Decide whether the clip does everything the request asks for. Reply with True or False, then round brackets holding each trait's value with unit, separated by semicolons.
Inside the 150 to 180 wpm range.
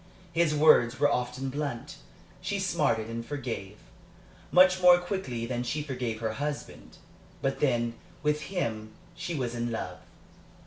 False (140 wpm)